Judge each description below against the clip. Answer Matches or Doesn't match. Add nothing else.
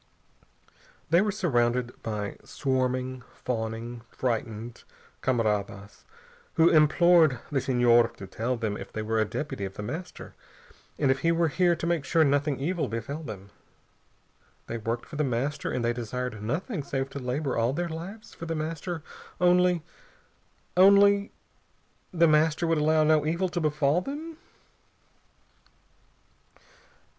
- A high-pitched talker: Doesn't match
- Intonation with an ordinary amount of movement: Doesn't match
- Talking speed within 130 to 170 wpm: Matches